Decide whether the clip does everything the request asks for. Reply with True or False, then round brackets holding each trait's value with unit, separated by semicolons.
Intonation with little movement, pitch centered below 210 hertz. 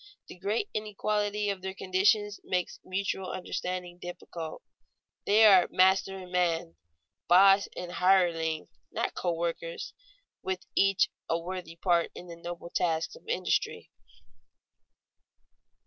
True (2.3 semitones; 185 Hz)